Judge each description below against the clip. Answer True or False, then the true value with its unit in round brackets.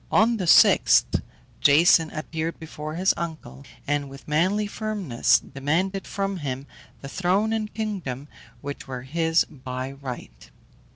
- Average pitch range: False (5.7 semitones)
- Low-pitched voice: False (160 Hz)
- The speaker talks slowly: True (130 wpm)